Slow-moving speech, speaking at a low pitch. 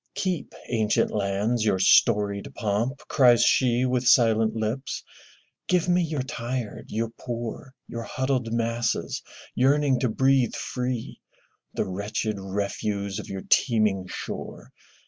Yes: slow, 125 wpm; low, 115 Hz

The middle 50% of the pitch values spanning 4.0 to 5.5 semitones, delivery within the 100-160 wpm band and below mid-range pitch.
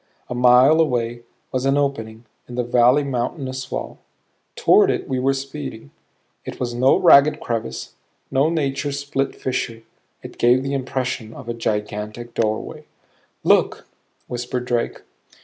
No: narrow, 2.5 semitones; average, 140 wpm; low, 125 Hz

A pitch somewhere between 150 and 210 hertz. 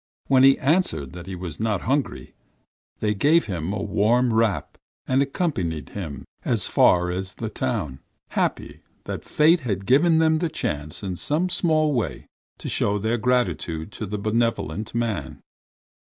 No: low, 110 Hz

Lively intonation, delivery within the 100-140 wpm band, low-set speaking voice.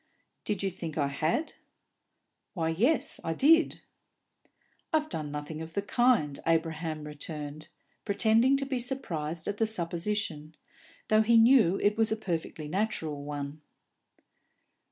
No: wide, 6.2 semitones; slow, 135 wpm; medium, 170 Hz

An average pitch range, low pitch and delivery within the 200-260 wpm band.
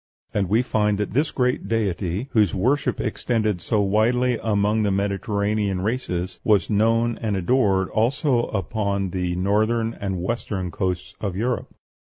No: average, 3.0 semitones; low, 105 Hz; average, 145 wpm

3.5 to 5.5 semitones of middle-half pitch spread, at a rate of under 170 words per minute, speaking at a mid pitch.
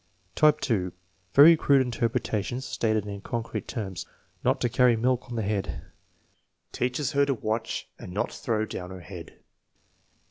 No: average, 3.8 semitones; average, 150 wpm; low, 115 Hz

